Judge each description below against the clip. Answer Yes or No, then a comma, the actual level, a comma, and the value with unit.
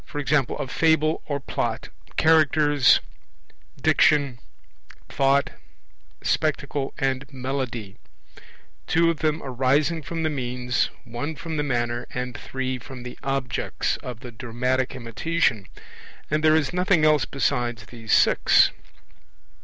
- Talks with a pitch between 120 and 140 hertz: Yes, low, 135 Hz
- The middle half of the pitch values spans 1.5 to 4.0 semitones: Yes, average, 3.6 semitones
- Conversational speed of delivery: No, slow, 115 wpm